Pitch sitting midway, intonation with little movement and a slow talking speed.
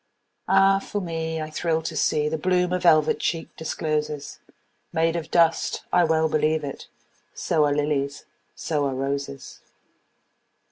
Yes: medium, 160 Hz; narrow, 2.0 semitones; slow, 125 wpm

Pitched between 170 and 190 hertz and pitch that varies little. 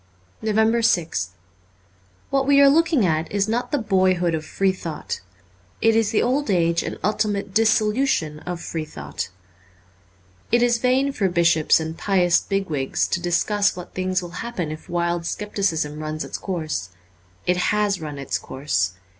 No: medium, 185 Hz; average, 5.2 semitones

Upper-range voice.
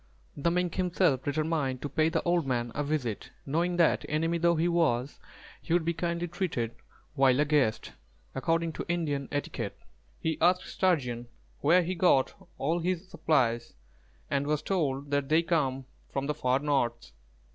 No: medium, 155 Hz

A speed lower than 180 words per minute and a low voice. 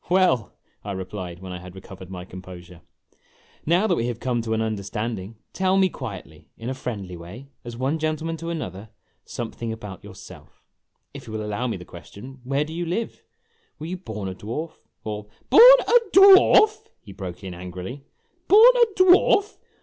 No: average, 190 wpm; low, 115 Hz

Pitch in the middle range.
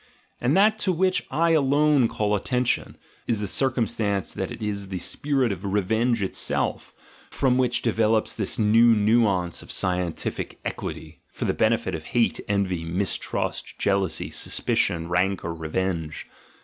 No: low, 105 Hz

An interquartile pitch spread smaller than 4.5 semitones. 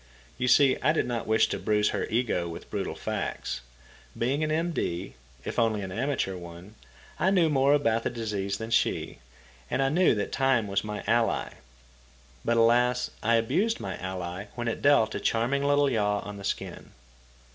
No: average, 4.9 semitones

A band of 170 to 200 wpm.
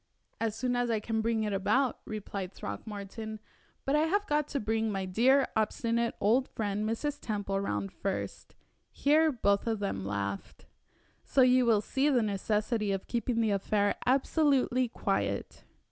No: average, 160 wpm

